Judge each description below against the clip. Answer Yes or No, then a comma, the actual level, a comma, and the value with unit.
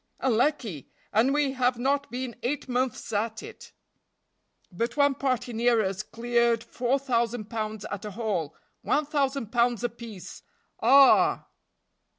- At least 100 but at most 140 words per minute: Yes, slow, 135 wpm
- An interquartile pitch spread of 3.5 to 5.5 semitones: No, average, 3.1 semitones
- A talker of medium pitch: No, high, 240 Hz